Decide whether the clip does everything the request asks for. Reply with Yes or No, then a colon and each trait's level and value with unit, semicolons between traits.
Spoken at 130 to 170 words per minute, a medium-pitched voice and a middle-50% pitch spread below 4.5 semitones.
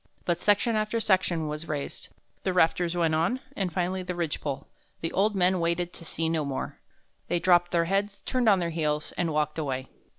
No: average, 200 wpm; medium, 175 Hz; average, 2.8 semitones